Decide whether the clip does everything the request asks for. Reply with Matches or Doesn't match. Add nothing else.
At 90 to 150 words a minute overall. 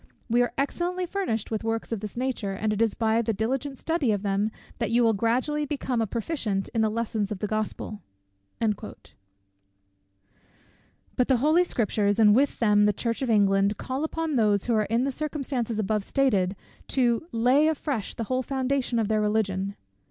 Doesn't match